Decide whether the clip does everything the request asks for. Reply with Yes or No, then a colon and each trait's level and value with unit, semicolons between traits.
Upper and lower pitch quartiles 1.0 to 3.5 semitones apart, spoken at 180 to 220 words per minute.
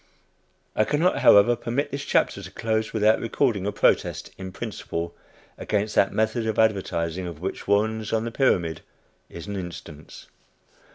No: average, 3.2 semitones; average, 155 wpm